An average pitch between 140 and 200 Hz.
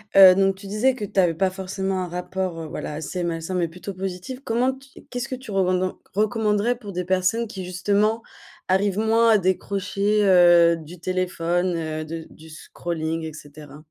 Yes: medium, 185 Hz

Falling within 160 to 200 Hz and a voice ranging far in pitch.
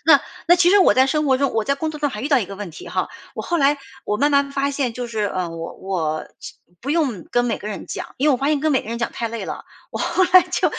No: very high, 265 Hz; wide, 5.7 semitones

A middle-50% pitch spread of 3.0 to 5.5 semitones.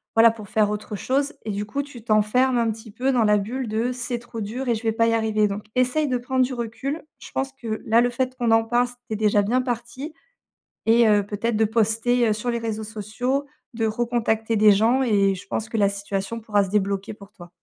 No: narrow, 2.6 semitones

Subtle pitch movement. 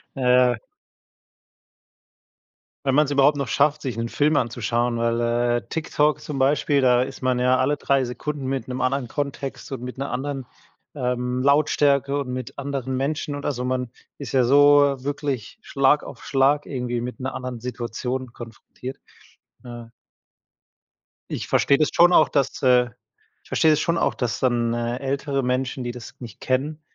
Yes: narrow, 2.3 semitones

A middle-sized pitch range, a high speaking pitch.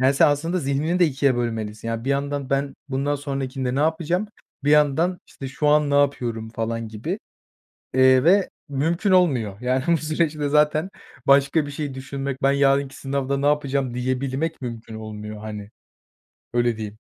No: average, 3.1 semitones; medium, 140 Hz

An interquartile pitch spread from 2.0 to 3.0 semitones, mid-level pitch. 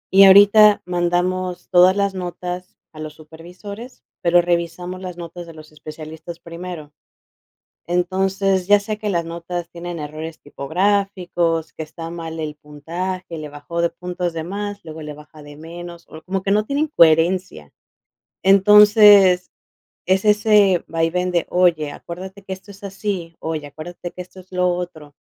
Yes: average, 2.7 semitones; medium, 175 Hz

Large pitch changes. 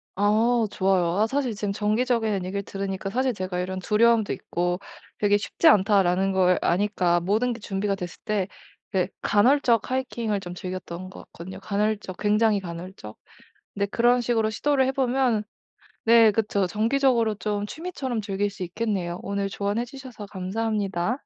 No: average, 3.4 semitones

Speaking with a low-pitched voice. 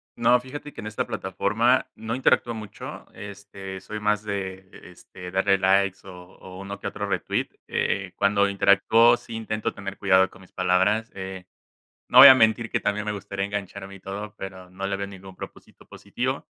Yes: low, 100 Hz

